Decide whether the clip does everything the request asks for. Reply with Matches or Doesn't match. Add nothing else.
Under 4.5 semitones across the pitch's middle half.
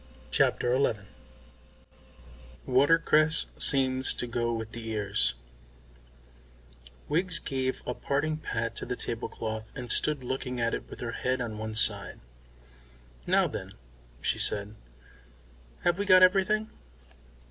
Doesn't match